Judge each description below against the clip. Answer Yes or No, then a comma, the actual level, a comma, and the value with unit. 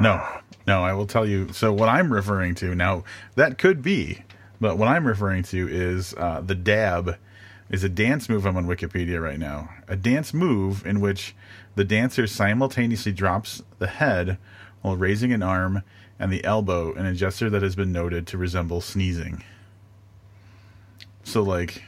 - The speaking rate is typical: Yes, average, 175 wpm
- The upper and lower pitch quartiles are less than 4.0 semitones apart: Yes, narrow, 2.5 semitones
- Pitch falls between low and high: No, low, 100 Hz